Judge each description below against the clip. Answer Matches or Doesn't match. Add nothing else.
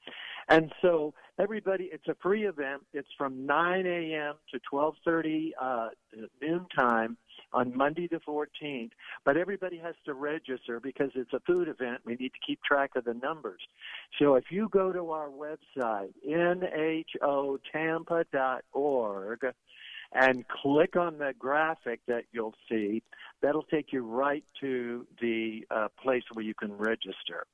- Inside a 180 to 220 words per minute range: Doesn't match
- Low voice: Doesn't match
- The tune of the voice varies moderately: Matches